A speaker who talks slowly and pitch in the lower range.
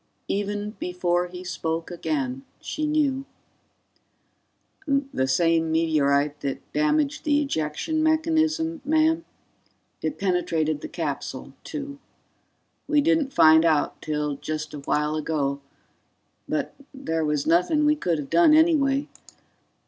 No: slow, 120 wpm; medium, 180 Hz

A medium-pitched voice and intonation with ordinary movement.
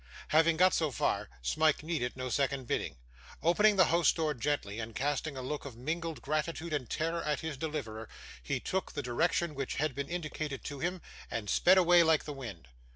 Yes: medium, 150 Hz; average, 4.1 semitones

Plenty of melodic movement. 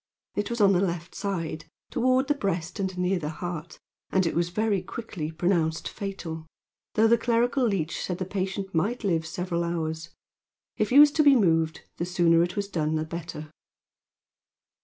No: average, 3.8 semitones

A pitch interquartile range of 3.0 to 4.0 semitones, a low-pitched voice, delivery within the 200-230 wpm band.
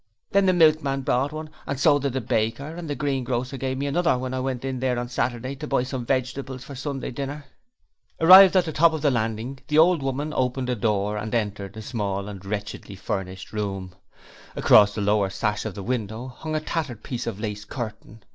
No: average, 4.8 semitones; low, 130 Hz; fast, 205 wpm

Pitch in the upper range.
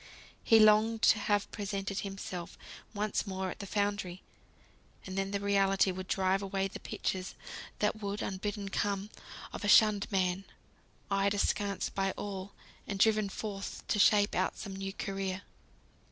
Yes: high, 200 Hz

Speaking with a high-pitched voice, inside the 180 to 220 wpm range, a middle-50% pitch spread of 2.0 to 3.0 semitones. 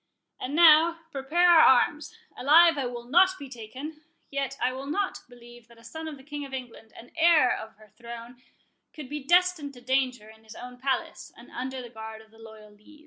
No: very high, 265 Hz; fast, 205 wpm; average, 4.4 semitones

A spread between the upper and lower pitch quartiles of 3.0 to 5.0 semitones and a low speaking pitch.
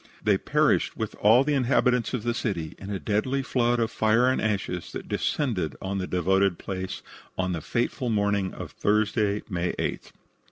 Yes: average, 4.1 semitones; low, 105 Hz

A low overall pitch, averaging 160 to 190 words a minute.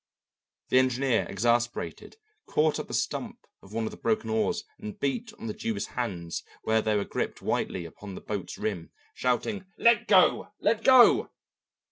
Yes: low, 125 Hz; average, 165 wpm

